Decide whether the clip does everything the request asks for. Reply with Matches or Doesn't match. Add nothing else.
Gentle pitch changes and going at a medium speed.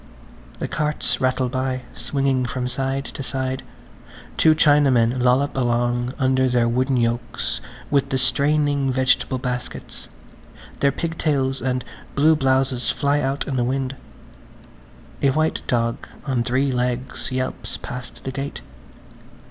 Doesn't match